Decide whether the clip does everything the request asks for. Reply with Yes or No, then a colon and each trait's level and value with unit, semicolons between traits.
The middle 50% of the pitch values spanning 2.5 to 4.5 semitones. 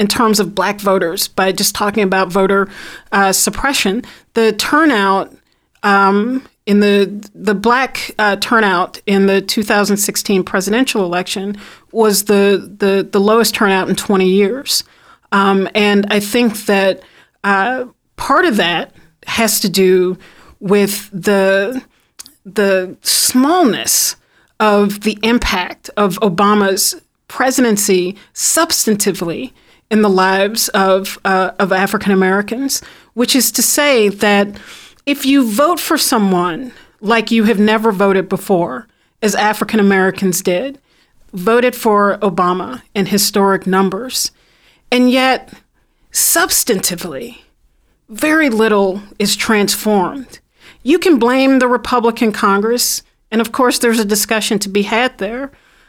Yes: average, 3.3 semitones